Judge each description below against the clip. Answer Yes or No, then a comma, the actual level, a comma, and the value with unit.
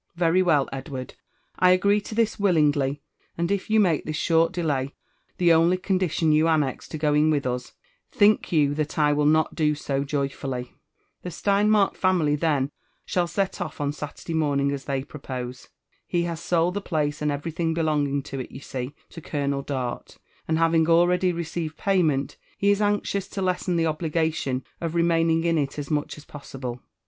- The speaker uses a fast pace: No, average, 175 wpm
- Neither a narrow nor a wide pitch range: Yes, average, 3.5 semitones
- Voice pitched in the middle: Yes, medium, 155 Hz